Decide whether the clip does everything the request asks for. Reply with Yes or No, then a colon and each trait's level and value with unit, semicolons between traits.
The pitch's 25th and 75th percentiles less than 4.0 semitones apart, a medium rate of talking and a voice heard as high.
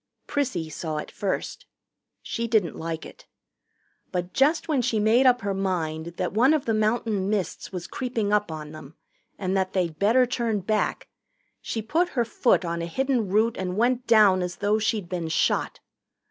No: average, 4.8 semitones; average, 180 wpm; high, 205 Hz